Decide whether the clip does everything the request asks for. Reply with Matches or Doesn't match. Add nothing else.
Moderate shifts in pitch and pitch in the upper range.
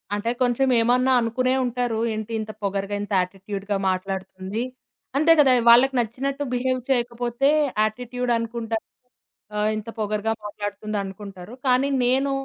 Matches